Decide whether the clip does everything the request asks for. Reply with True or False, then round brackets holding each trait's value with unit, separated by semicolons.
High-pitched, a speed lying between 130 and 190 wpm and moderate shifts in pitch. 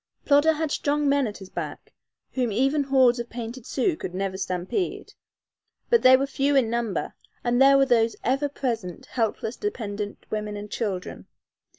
True (245 Hz; 170 wpm; 4.7 semitones)